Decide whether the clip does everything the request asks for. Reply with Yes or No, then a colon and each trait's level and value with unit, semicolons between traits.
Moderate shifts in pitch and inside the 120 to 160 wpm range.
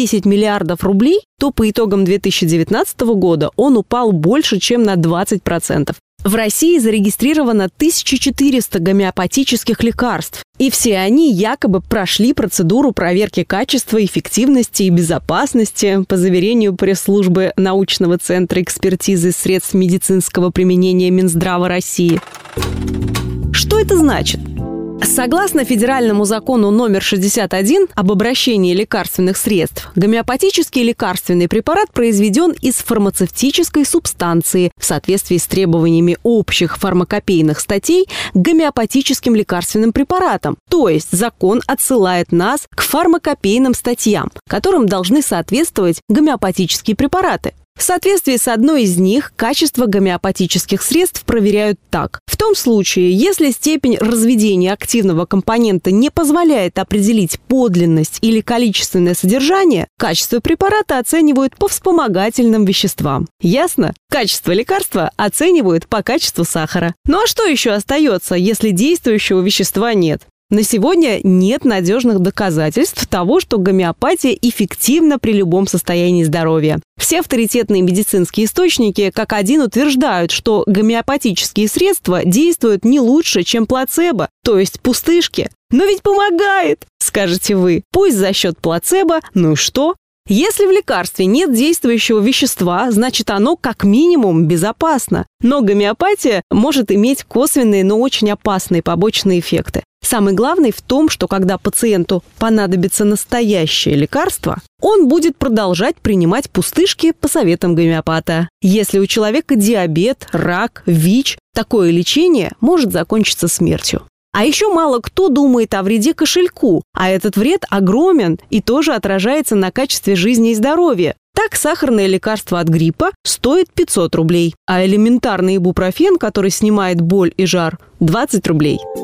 No: wide, 6.4 semitones; average, 125 wpm